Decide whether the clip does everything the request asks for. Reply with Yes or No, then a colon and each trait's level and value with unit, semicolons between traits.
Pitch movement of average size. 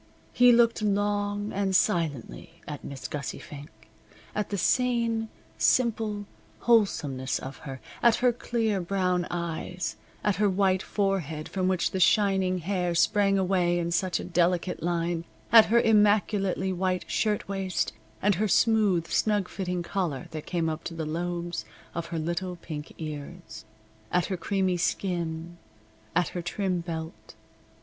Yes: average, 3.3 semitones